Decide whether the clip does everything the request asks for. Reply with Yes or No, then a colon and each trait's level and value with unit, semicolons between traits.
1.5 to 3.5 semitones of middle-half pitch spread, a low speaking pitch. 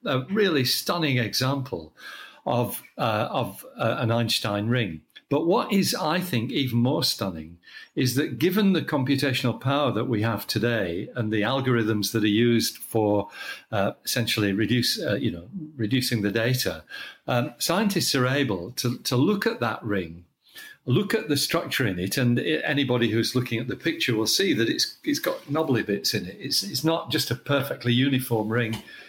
No: average, 4.1 semitones; low, 125 Hz